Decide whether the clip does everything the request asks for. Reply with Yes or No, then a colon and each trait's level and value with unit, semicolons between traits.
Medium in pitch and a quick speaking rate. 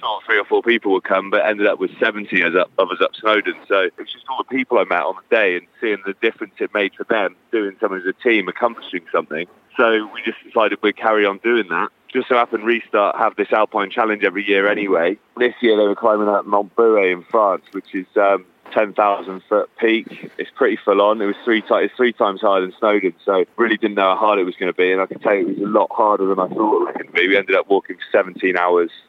No: low, 105 Hz; fast, 265 wpm